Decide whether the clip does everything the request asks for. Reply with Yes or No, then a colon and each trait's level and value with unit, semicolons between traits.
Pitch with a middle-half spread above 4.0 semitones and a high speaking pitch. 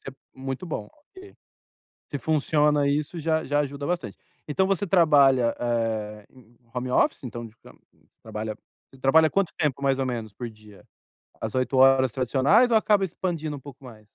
No: average, 4.8 semitones; low, 135 Hz